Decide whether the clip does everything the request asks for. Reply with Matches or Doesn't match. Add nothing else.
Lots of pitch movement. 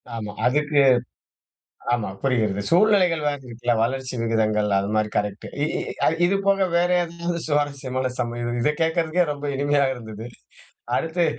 Matches